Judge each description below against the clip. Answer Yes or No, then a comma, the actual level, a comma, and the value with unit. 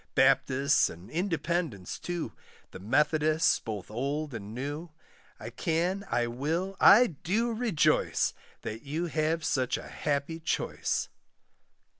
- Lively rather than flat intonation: No, average, 4.9 semitones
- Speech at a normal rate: No, slow, 120 wpm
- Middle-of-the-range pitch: Yes, medium, 155 Hz